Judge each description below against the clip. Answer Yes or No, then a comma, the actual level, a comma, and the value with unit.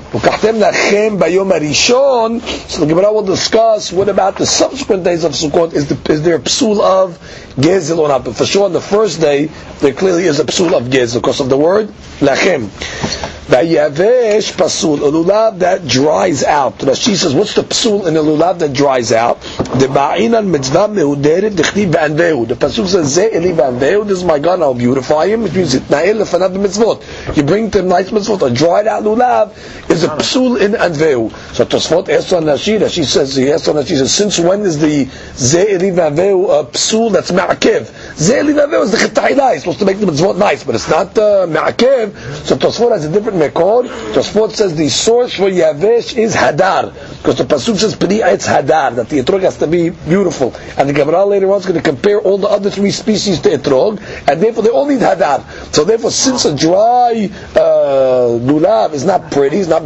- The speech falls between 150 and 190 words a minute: Yes, average, 170 wpm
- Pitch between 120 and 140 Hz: No, high, 195 Hz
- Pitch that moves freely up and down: Yes, wide, 5.7 semitones